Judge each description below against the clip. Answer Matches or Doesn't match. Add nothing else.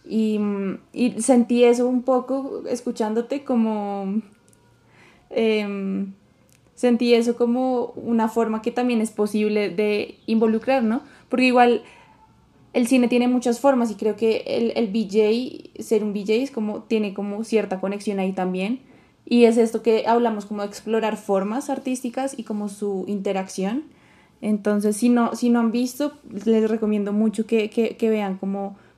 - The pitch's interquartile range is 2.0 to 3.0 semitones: Matches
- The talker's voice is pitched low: Doesn't match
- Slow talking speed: Doesn't match